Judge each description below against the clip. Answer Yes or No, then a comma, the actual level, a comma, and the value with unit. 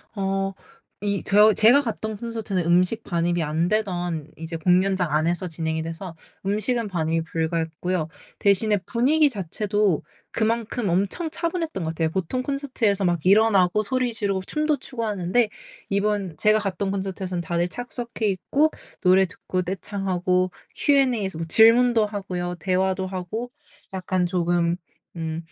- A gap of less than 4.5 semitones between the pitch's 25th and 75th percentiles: Yes, average, 3.8 semitones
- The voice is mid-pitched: No, high, 195 Hz